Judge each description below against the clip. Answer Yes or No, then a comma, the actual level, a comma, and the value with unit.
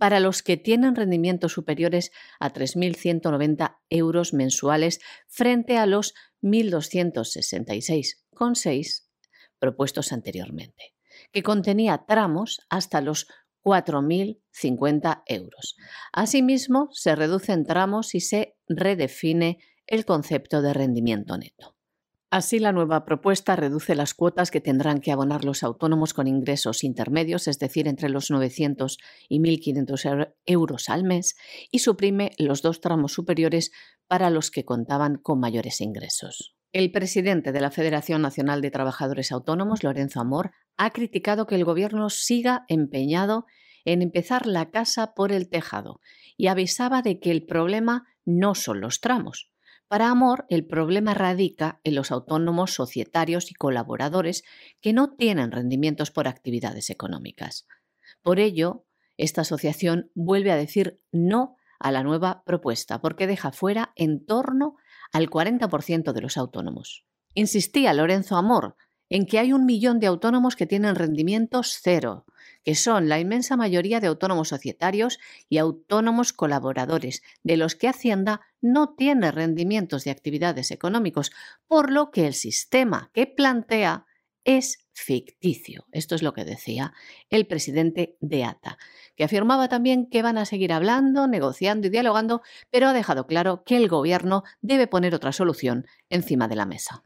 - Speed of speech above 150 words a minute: No, average, 140 wpm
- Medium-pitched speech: Yes, medium, 175 Hz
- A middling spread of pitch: No, wide, 6.3 semitones